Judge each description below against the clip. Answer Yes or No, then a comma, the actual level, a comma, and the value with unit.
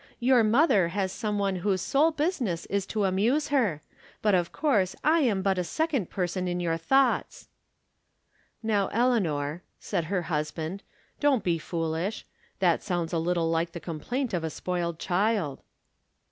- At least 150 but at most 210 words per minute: Yes, average, 165 wpm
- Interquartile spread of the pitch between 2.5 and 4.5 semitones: No, average, 5.2 semitones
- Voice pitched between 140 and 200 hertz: Yes, high, 190 Hz